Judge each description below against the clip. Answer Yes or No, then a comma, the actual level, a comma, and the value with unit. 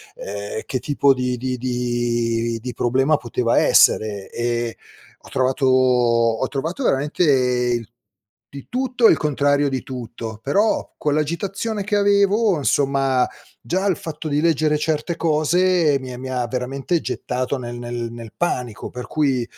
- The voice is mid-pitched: No, low, 130 Hz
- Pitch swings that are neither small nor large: Yes, average, 4.4 semitones